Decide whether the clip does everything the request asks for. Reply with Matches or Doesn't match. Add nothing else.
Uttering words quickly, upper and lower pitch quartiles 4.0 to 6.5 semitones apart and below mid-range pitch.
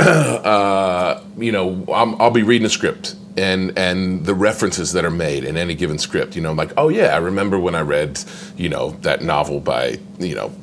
Doesn't match